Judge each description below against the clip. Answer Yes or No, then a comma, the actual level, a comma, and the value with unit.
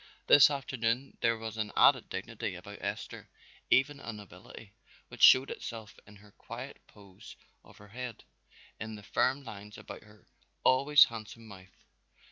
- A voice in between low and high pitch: No, low, 110 Hz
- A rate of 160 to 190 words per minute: No, average, 150 wpm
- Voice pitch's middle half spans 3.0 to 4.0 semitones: Yes, average, 3.7 semitones